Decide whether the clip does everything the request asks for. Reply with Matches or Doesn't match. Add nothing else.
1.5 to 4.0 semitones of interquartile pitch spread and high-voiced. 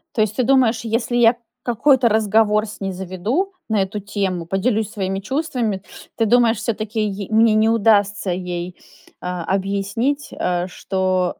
Matches